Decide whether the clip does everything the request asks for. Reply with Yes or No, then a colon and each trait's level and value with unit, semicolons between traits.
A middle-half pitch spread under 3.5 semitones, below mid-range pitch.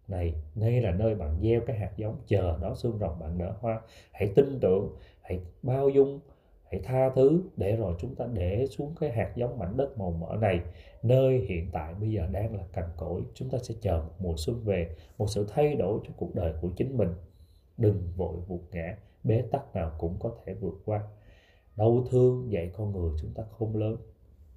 No: average, 4.9 semitones; low, 100 Hz